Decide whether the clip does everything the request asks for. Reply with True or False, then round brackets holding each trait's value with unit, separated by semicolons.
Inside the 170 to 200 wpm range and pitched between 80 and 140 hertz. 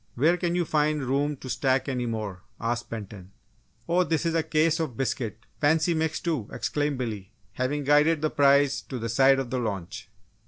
True (190 wpm; 135 Hz)